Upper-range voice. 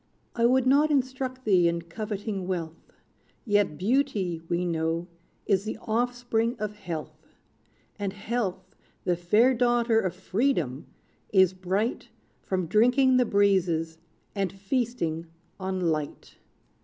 Yes: high, 200 Hz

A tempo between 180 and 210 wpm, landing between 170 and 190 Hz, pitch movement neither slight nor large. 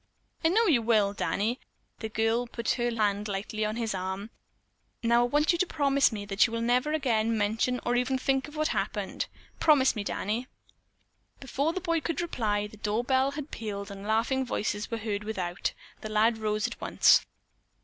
No: average, 190 wpm; high, 230 Hz; average, 3.9 semitones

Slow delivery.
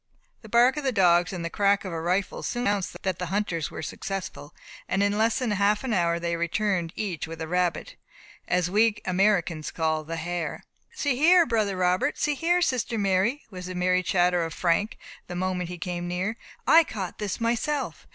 No: average, 195 wpm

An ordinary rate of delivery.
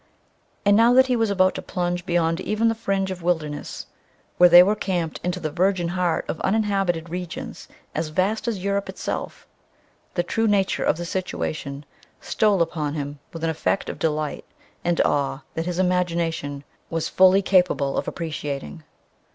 Yes: average, 165 wpm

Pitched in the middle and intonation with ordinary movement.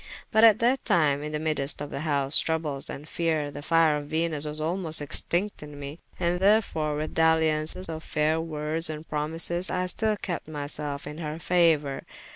No: medium, 155 Hz; narrow, 2.2 semitones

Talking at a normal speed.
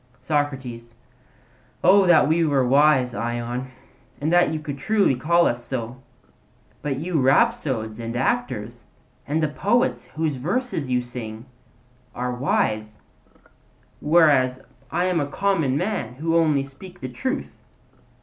No: slow, 130 wpm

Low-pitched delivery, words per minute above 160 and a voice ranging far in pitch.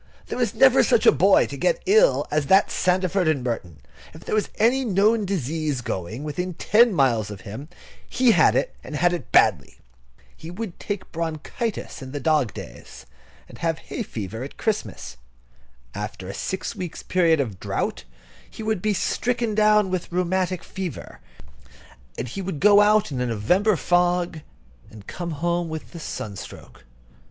No: medium, 175 Hz; average, 170 wpm; wide, 7.2 semitones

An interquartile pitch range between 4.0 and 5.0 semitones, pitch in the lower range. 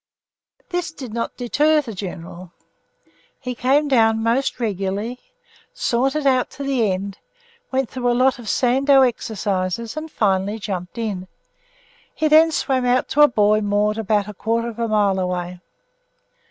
No: average, 4.5 semitones; high, 230 Hz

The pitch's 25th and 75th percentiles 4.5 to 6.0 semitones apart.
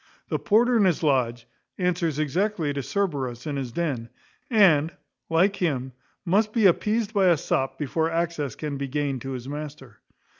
Yes: wide, 5.6 semitones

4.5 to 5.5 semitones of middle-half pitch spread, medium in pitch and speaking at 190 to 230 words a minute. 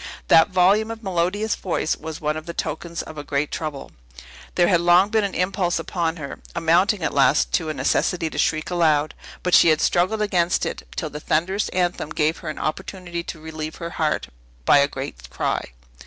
No: average, 2.9 semitones; medium, 170 Hz; average, 200 wpm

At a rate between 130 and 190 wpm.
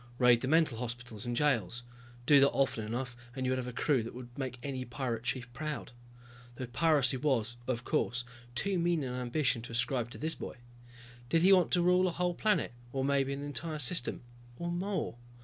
No: average, 200 wpm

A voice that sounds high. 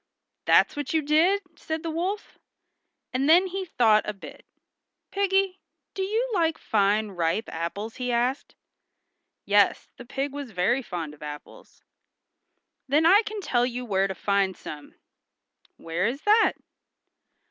Yes: very high, 255 Hz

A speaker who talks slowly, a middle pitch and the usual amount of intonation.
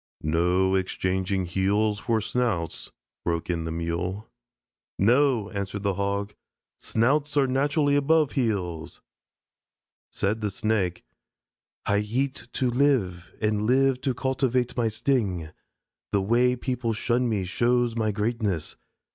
No: slow, 120 wpm; low, 110 Hz; average, 4.9 semitones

